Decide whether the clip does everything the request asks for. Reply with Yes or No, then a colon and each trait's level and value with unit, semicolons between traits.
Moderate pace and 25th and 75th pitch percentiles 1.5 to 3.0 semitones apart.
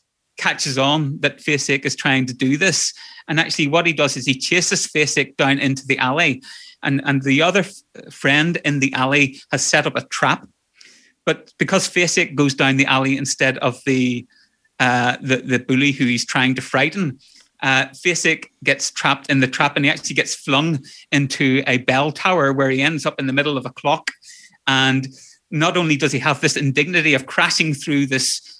Yes: average, 195 wpm; average, 2.7 semitones